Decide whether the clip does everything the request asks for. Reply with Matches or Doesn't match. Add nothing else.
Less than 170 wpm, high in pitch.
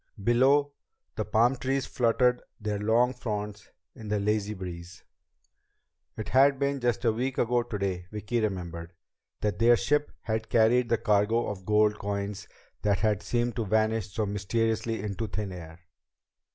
Doesn't match